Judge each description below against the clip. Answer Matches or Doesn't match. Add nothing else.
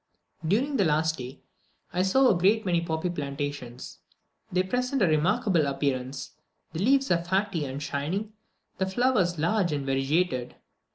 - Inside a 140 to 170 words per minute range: Matches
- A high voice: Doesn't match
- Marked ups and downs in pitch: Matches